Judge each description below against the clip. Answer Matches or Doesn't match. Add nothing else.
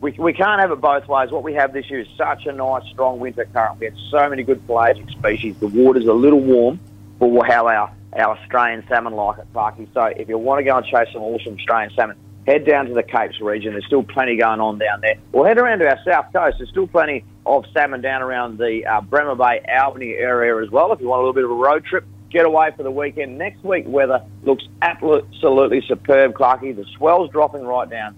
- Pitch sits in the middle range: Doesn't match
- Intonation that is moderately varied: Matches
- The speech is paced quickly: Matches